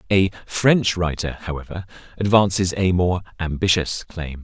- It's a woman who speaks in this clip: No, male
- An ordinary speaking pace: No, slow, 120 wpm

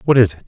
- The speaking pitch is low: Yes, low, 110 Hz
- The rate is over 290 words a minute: Yes, fast, 375 wpm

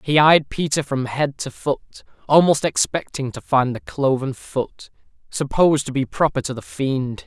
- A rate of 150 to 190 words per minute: Yes, average, 175 wpm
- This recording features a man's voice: Yes, male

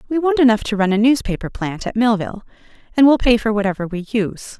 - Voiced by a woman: Yes, female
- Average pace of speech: No, fast, 220 wpm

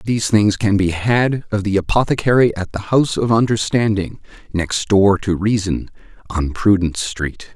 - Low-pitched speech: Yes, low, 105 Hz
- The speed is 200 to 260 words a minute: No, average, 160 wpm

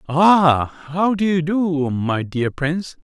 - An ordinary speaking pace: Yes, average, 155 wpm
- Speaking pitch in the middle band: Yes, medium, 160 Hz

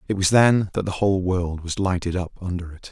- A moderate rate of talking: No, fast, 245 wpm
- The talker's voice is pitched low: Yes, very low, 95 Hz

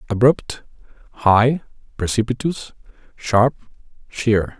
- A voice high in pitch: No, low, 115 Hz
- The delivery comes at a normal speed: No, slow, 65 wpm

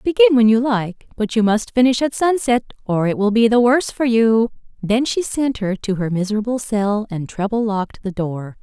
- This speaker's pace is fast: Yes, fast, 215 wpm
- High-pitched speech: Yes, high, 225 Hz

